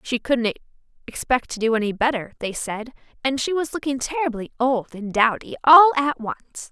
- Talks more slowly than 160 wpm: No, average, 180 wpm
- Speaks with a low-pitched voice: No, very high, 250 Hz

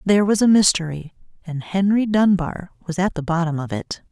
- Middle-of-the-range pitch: Yes, medium, 180 Hz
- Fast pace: No, average, 190 wpm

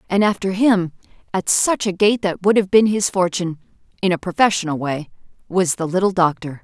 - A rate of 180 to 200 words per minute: Yes, average, 190 wpm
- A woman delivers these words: Yes, female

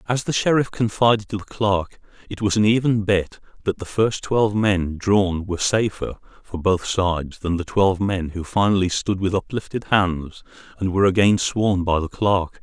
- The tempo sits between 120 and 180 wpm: No, average, 190 wpm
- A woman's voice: No, male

